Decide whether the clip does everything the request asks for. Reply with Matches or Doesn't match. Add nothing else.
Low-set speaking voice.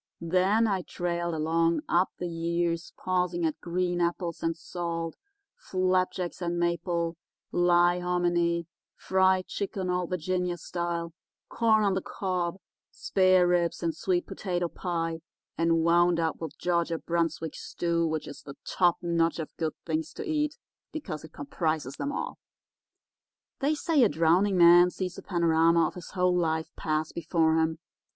Doesn't match